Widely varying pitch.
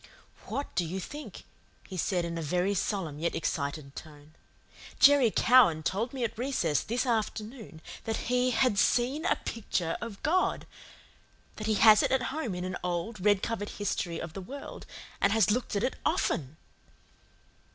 Yes: wide, 6.1 semitones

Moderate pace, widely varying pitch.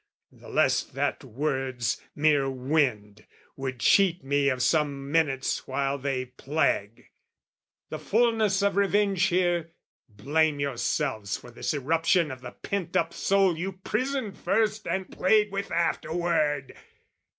No: slow, 130 wpm; wide, 6.1 semitones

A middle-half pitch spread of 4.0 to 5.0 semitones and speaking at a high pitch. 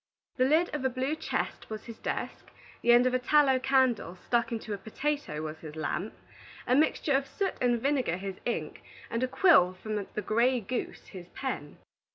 Yes: average, 4.7 semitones; high, 245 Hz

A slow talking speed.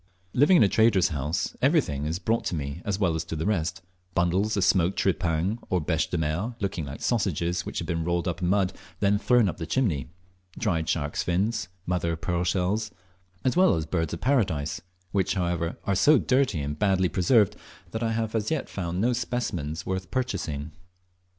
No: average, 200 wpm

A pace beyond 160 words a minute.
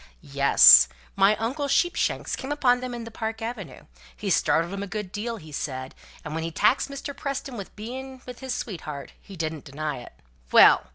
Yes: average, 190 wpm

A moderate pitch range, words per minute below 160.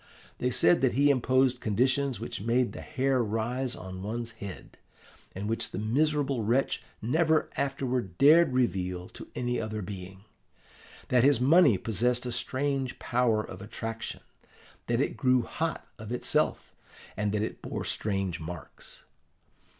Yes: average, 3.9 semitones; average, 145 wpm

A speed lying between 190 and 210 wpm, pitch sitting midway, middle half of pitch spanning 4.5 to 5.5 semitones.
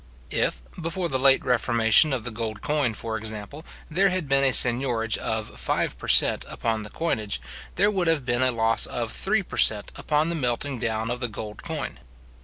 No: average, 200 wpm; low, 125 Hz; average, 5.1 semitones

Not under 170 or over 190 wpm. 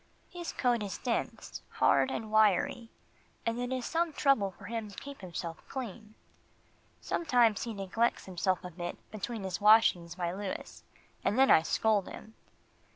No: average, 155 wpm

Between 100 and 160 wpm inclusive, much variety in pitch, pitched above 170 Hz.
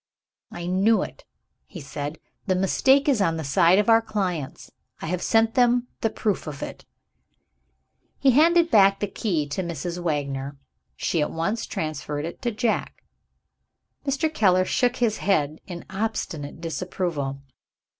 Yes: average, 150 wpm; wide, 6.0 semitones; medium, 185 Hz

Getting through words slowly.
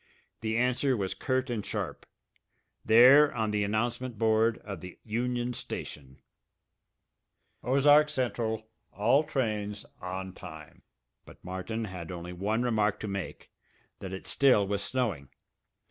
Yes: slow, 130 wpm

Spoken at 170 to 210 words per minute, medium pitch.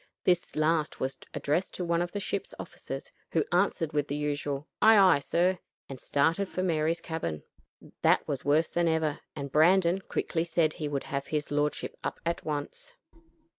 Yes: average, 175 wpm; medium, 160 Hz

